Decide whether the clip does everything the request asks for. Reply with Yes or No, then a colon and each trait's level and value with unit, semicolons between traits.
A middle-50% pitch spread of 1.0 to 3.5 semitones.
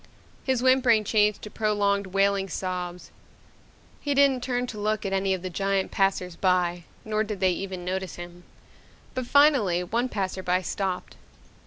Yes: average, 3.0 semitones